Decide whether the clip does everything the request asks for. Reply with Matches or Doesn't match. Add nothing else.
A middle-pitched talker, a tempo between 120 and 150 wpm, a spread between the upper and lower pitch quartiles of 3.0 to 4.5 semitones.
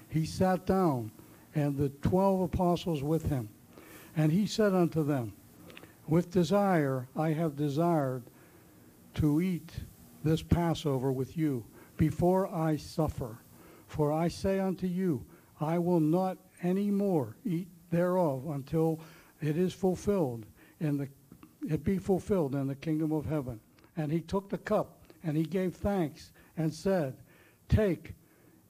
Matches